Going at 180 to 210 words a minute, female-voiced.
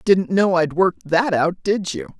No: fast, 220 wpm; female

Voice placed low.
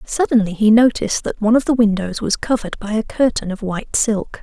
No: high, 220 Hz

